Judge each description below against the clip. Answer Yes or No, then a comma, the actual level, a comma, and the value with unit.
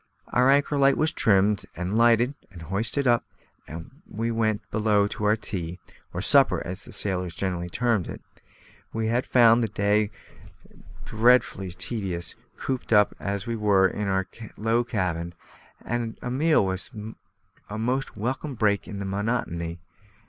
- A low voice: Yes, low, 105 Hz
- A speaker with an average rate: Yes, average, 150 wpm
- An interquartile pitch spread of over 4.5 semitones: No, average, 3.8 semitones